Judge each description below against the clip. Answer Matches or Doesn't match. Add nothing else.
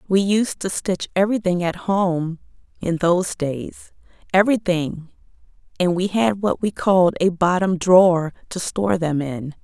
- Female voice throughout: Matches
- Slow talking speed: Doesn't match